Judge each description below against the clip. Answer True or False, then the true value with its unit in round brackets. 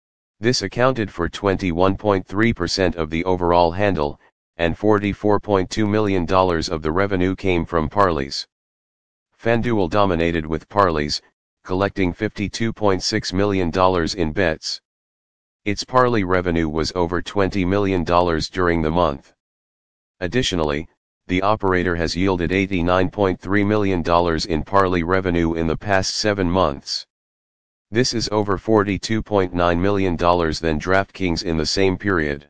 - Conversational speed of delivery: False (115 wpm)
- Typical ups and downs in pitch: True (3.0 semitones)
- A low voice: True (95 Hz)